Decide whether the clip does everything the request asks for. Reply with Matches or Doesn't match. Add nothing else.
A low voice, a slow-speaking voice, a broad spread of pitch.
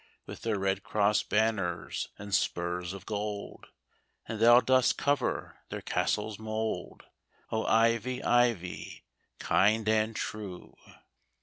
Doesn't match